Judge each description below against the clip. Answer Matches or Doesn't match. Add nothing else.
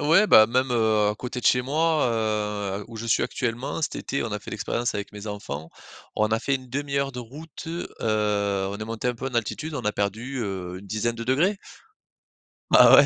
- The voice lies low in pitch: Matches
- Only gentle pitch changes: Doesn't match